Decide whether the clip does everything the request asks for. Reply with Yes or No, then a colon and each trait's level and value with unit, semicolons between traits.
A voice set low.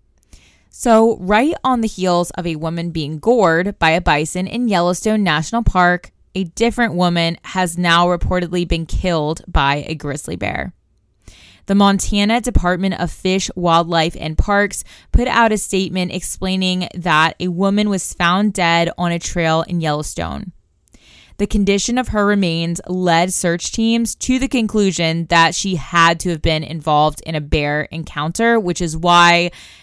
No: medium, 175 Hz